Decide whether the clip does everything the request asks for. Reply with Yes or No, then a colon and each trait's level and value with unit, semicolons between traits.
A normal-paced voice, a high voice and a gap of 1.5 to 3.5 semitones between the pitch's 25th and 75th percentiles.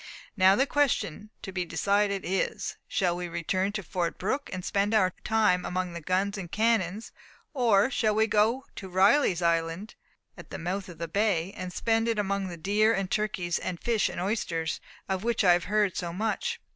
Yes: average, 195 wpm; high, 195 Hz; average, 3.2 semitones